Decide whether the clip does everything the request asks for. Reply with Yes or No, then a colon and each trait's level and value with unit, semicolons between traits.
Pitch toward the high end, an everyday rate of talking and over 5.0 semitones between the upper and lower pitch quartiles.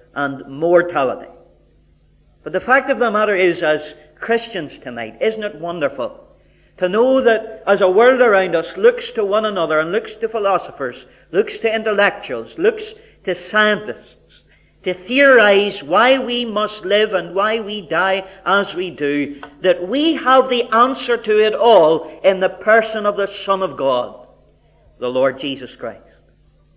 Yes: high, 200 Hz; average, 155 wpm; wide, 5.5 semitones